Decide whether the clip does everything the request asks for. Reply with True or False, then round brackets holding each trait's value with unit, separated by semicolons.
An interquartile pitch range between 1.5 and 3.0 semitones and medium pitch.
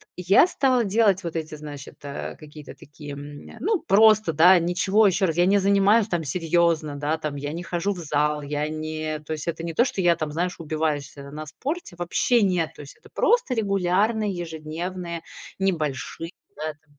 False (4.2 semitones; 170 Hz)